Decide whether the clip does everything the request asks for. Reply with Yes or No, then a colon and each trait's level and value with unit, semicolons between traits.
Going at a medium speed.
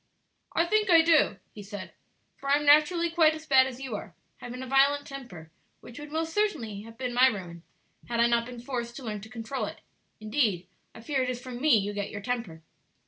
No: fast, 225 wpm